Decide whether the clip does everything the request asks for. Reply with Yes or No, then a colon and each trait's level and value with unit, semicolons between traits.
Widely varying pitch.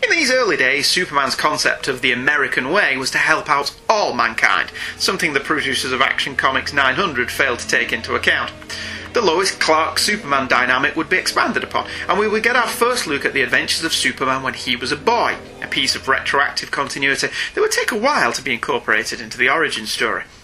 Yes: wide, 8.5 semitones